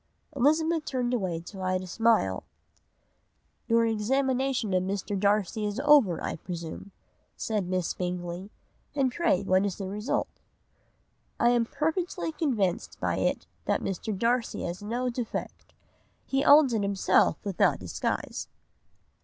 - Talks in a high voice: Yes, high, 215 Hz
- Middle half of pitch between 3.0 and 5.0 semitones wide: No, wide, 5.6 semitones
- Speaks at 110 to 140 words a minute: Yes, slow, 135 wpm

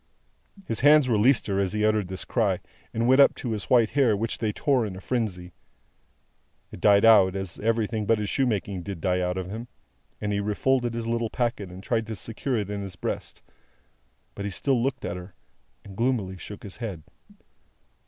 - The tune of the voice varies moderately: Yes, average, 3.3 semitones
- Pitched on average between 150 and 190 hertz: No, low, 105 Hz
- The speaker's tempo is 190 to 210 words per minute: Yes, average, 200 wpm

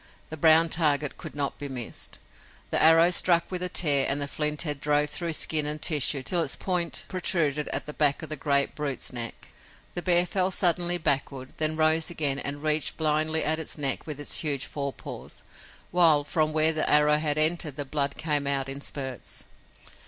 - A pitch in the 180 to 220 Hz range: No, medium, 150 Hz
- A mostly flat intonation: Yes, narrow, 2.3 semitones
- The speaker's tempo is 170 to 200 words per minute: Yes, average, 195 wpm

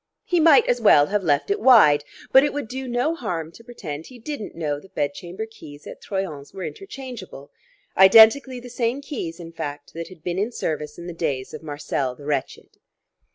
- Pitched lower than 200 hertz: Yes, high, 190 Hz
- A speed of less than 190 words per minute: No, average, 200 wpm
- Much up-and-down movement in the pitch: Yes, wide, 8.6 semitones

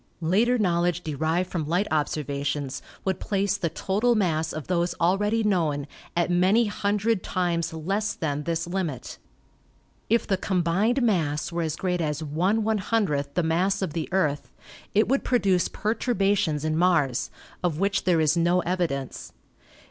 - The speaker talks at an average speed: Yes, average, 150 wpm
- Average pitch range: Yes, average, 4.0 semitones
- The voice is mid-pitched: Yes, medium, 175 Hz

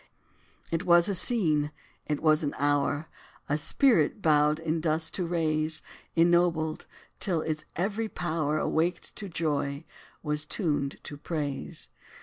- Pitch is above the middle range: No, medium, 160 Hz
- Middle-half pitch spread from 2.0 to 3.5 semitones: Yes, narrow, 2.4 semitones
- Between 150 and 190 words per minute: No, slow, 135 wpm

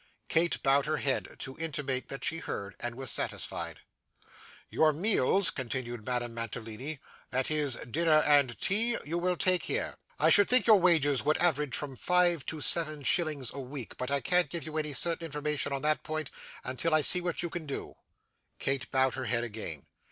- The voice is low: No, medium, 150 Hz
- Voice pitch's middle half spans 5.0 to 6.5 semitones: No, average, 4.1 semitones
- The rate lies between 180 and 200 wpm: Yes, average, 190 wpm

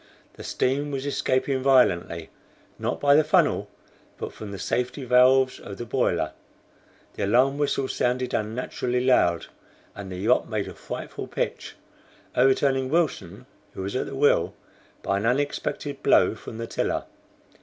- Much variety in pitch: No, average, 4.0 semitones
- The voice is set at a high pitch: No, low, 125 Hz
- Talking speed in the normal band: Yes, average, 150 wpm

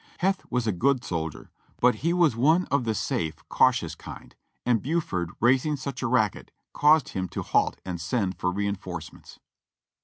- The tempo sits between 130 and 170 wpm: Yes, average, 165 wpm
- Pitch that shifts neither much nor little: No, wide, 7.3 semitones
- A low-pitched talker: Yes, low, 120 Hz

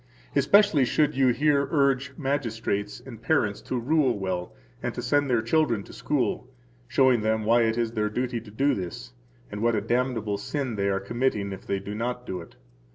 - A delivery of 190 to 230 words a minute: Yes, average, 195 wpm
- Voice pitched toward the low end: Yes, low, 120 Hz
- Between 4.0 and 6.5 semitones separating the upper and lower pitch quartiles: Yes, average, 4.4 semitones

